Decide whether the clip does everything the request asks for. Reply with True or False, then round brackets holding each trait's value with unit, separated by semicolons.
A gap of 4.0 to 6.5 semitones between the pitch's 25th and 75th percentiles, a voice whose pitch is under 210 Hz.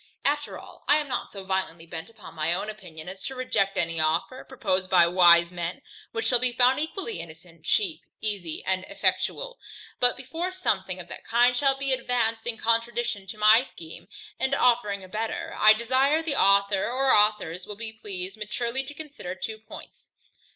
False (5.5 semitones; 215 Hz)